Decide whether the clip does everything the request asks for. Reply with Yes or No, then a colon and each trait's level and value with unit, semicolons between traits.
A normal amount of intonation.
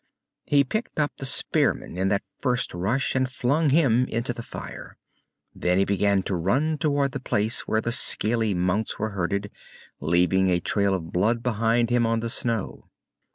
Yes: average, 4.8 semitones